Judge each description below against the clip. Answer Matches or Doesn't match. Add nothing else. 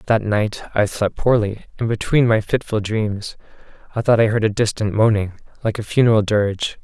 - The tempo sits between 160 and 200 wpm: Matches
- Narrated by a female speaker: Doesn't match